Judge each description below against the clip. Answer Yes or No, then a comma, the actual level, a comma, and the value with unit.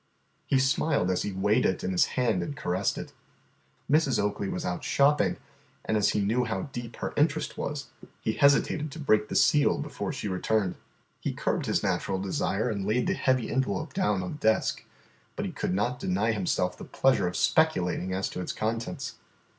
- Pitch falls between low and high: No, low, 110 Hz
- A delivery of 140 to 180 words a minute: No, average, 195 wpm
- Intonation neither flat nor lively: No, wide, 6.1 semitones